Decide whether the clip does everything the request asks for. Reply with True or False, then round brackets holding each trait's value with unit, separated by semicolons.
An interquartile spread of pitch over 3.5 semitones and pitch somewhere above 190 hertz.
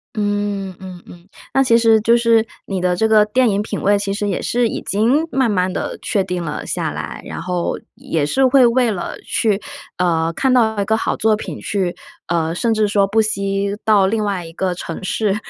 False (3.2 semitones; 205 Hz)